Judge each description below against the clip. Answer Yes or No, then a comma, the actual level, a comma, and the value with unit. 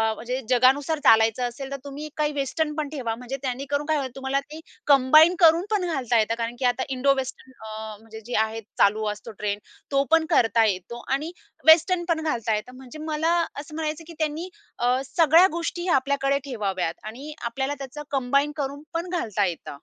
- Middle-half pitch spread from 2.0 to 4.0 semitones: No, average, 4.5 semitones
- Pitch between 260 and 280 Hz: Yes, very high, 275 Hz